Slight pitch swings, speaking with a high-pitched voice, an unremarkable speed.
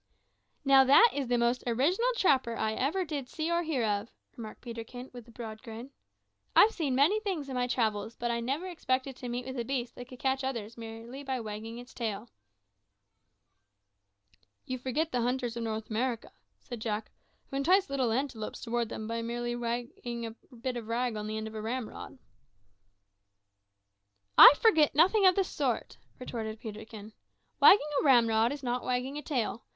No: average, 3.1 semitones; high, 245 Hz; average, 180 wpm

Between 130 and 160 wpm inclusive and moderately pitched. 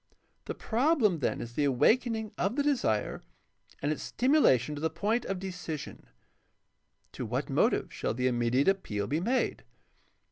Yes: average, 150 wpm; medium, 175 Hz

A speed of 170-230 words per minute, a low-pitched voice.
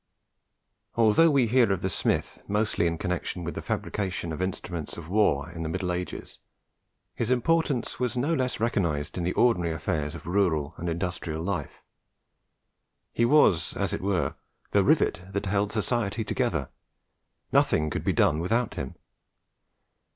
No: average, 155 wpm; very low, 95 Hz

